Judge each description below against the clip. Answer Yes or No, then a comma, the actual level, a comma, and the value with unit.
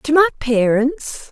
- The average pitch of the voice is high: Yes, very high, 265 Hz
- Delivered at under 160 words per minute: Yes, slow, 135 wpm